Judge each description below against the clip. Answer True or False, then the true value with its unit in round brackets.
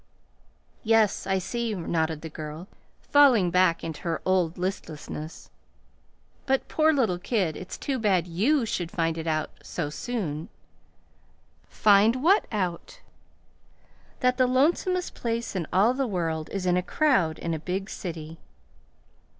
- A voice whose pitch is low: False (185 Hz)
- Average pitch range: False (6.3 semitones)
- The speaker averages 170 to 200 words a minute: False (140 wpm)